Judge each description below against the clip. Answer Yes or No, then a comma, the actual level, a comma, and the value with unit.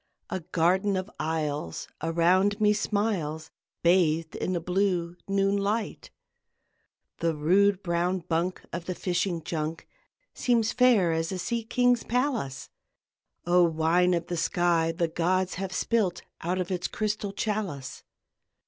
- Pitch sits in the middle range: Yes, medium, 180 Hz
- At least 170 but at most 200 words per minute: No, slow, 135 wpm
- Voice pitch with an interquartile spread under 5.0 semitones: Yes, average, 3.4 semitones